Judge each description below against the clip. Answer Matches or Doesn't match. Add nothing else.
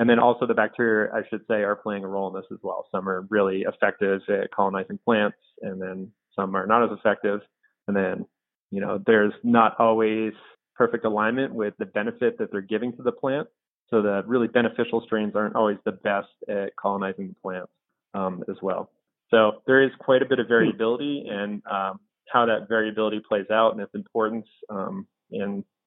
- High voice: Doesn't match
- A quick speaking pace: Doesn't match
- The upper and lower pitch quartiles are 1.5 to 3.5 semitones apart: Matches